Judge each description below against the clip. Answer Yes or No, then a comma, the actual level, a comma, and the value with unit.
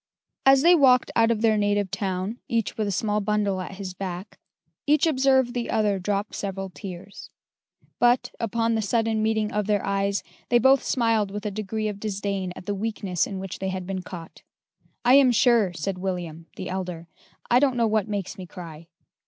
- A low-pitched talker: No, high, 205 Hz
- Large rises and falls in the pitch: No, average, 3.1 semitones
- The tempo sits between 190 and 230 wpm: Yes, average, 195 wpm